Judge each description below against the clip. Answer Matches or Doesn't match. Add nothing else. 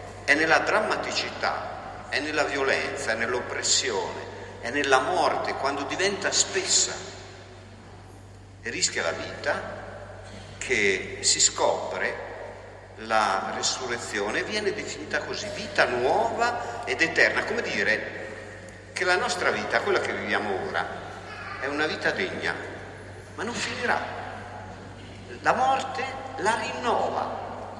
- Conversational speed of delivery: Doesn't match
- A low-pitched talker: Matches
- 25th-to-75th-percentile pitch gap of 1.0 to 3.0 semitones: Matches